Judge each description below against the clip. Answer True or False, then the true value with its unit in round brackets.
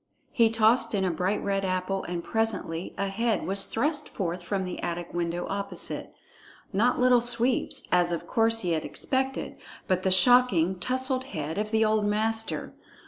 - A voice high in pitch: True (200 Hz)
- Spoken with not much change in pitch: False (4.2 semitones)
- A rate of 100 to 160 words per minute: False (170 wpm)